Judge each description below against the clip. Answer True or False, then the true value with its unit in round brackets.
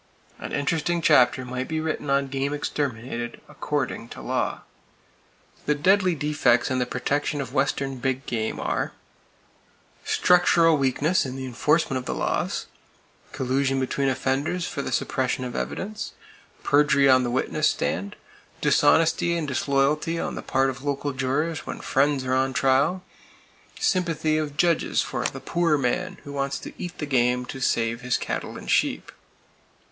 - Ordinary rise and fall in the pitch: True (3.0 semitones)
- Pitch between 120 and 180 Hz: True (140 Hz)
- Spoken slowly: False (155 wpm)